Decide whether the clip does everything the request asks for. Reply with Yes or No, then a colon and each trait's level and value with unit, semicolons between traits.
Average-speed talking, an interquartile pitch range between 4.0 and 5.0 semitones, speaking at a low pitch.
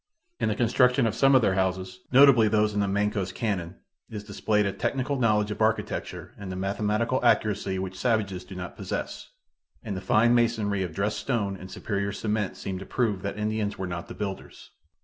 No: average, 195 wpm; narrow, 2.6 semitones; low, 105 Hz